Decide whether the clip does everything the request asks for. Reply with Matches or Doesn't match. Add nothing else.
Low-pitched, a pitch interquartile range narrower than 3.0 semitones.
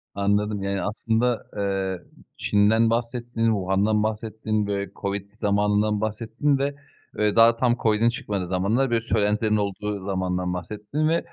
Matches